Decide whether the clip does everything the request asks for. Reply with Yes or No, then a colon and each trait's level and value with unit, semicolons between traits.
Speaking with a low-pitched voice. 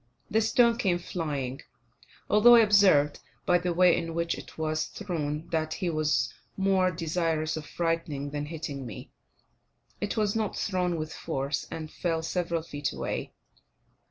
No: medium, 165 Hz